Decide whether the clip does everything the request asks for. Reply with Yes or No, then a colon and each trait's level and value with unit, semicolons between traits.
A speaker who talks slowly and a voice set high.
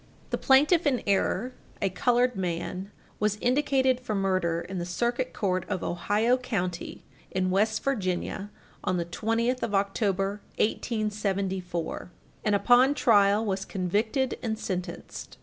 Yes: slow, 130 wpm; high, 205 Hz